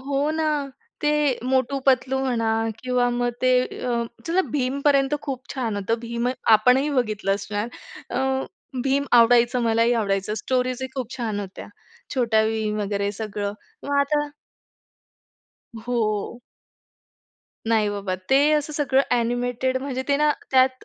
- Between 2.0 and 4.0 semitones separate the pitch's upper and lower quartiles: Yes, average, 3.4 semitones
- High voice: Yes, high, 245 Hz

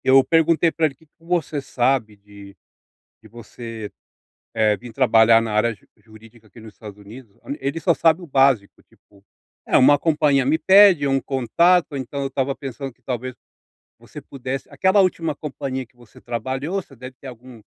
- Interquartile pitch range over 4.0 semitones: Yes, average, 4.4 semitones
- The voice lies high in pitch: No, low, 130 Hz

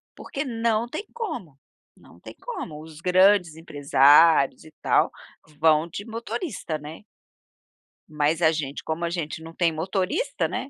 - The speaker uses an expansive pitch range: Yes, wide, 6.1 semitones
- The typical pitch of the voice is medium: Yes, medium, 165 Hz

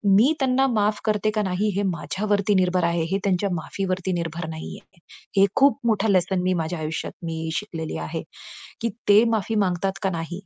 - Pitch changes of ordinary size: Yes, average, 3.6 semitones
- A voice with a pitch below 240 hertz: Yes, high, 190 Hz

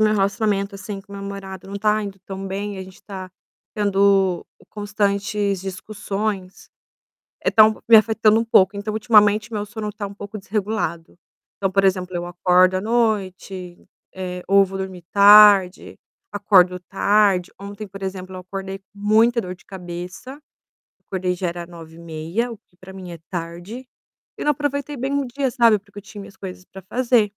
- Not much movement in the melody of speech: Yes, narrow, 2.3 semitones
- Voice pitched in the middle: No, high, 200 Hz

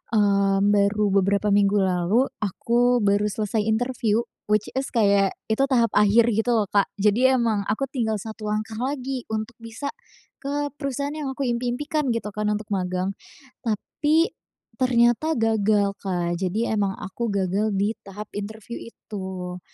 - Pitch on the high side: Yes, high, 215 Hz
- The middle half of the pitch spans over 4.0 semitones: No, average, 3.2 semitones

